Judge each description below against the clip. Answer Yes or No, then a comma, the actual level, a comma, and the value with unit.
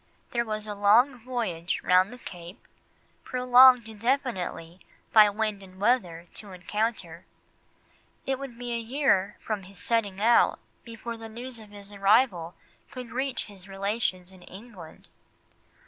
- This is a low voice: No, high, 215 Hz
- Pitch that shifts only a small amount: No, average, 3.9 semitones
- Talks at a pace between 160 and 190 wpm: No, average, 140 wpm